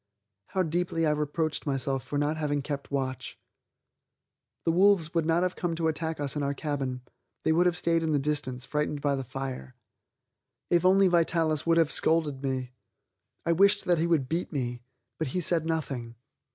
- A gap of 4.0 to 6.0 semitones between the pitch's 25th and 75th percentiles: No, average, 3.3 semitones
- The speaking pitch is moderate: Yes, medium, 155 Hz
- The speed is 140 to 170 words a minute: No, average, 185 wpm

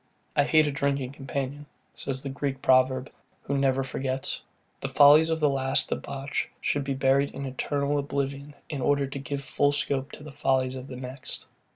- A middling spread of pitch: No, narrow, 1.2 semitones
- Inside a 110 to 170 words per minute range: No, average, 185 wpm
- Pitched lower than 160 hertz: Yes, medium, 140 Hz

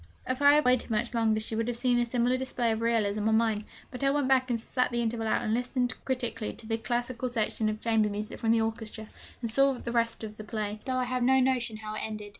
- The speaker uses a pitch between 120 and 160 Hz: No, high, 230 Hz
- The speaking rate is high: Yes, fast, 260 wpm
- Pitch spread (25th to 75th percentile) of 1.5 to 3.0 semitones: Yes, narrow, 2.4 semitones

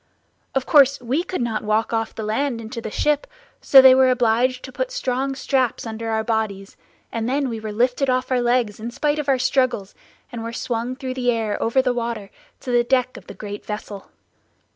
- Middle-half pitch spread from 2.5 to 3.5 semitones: Yes, average, 2.8 semitones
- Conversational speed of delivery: No, fast, 210 wpm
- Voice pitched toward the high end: Yes, high, 245 Hz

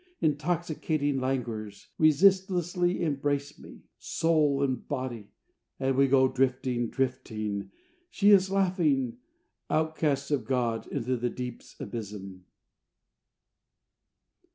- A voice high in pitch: No, low, 135 Hz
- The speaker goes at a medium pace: No, slow, 95 wpm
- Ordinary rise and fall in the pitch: Yes, average, 4.2 semitones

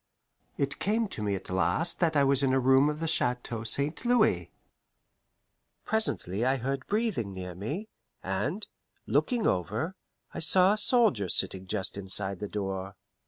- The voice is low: Yes, low, 130 Hz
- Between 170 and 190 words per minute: No, average, 160 wpm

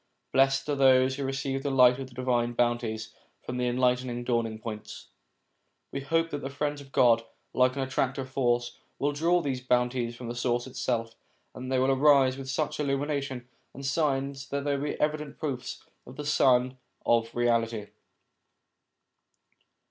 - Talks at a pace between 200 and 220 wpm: No, average, 170 wpm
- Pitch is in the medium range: No, low, 130 Hz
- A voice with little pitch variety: Yes, narrow, 2.3 semitones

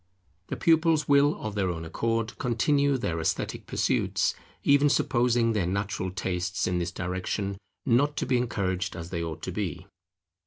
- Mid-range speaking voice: No, low, 105 Hz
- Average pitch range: No, wide, 6.2 semitones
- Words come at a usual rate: Yes, average, 160 wpm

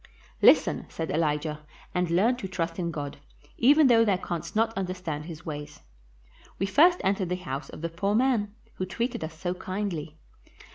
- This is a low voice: No, medium, 180 Hz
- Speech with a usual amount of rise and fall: Yes, average, 4.4 semitones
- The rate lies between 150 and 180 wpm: Yes, average, 175 wpm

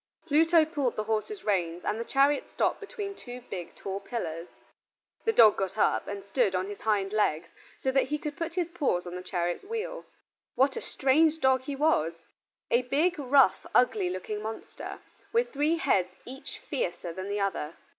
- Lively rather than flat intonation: Yes, wide, 7.5 semitones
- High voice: Yes, high, 245 Hz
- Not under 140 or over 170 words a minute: No, average, 185 wpm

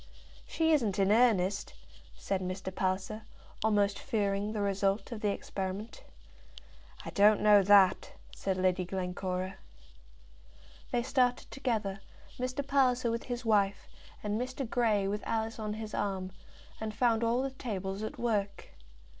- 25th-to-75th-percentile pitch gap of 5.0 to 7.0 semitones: No, average, 3.2 semitones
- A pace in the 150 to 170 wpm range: No, average, 140 wpm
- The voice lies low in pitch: No, high, 210 Hz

